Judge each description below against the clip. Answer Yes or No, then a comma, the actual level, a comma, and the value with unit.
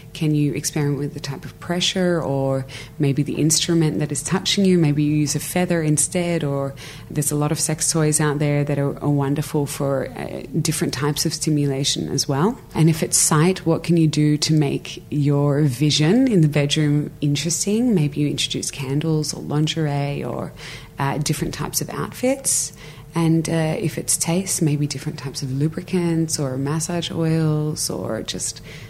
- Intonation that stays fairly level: Yes, narrow, 2.2 semitones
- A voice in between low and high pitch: Yes, medium, 150 Hz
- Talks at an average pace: Yes, average, 180 wpm